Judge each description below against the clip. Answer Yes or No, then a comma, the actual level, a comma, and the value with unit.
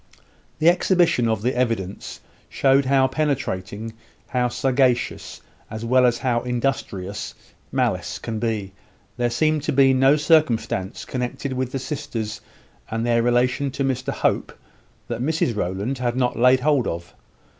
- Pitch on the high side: No, low, 125 Hz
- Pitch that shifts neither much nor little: Yes, average, 3.0 semitones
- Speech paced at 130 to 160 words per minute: Yes, average, 145 wpm